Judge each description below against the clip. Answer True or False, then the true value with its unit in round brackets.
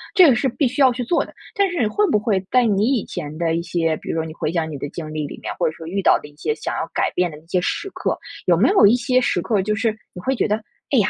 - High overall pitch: True (205 Hz)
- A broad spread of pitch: True (7.3 semitones)